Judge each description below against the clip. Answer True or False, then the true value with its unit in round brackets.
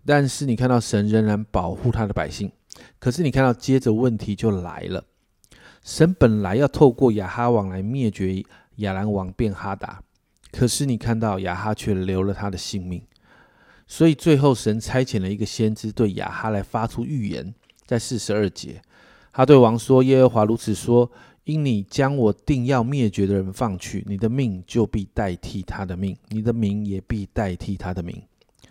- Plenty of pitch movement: False (3.8 semitones)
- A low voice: True (110 Hz)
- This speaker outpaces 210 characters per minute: True (260 characters per minute)